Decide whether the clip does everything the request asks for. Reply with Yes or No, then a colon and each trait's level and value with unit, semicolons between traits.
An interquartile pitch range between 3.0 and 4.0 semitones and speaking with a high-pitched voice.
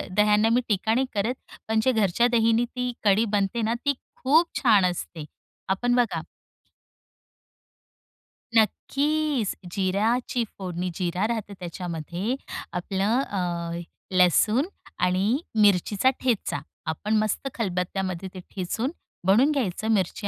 No: average, 4.5 semitones; high, 210 Hz